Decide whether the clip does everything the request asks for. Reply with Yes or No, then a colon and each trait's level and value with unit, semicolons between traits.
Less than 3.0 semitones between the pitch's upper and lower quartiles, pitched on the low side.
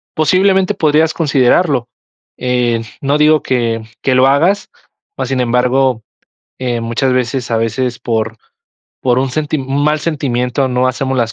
No: average, 3.5 semitones; low, 130 Hz